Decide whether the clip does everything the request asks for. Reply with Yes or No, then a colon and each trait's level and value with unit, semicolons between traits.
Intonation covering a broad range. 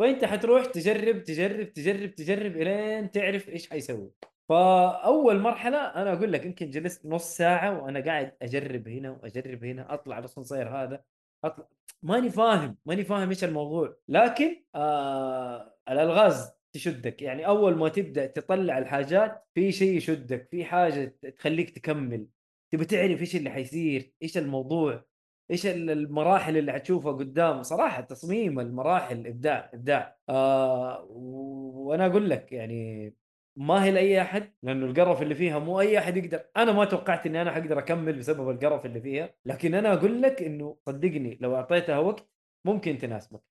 Yes: wide, 6.0 semitones